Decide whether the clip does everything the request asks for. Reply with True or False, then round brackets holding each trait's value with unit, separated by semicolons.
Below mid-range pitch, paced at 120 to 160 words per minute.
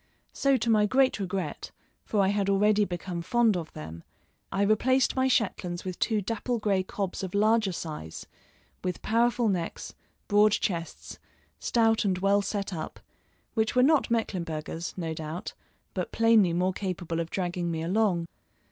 False (195 Hz; 155 wpm)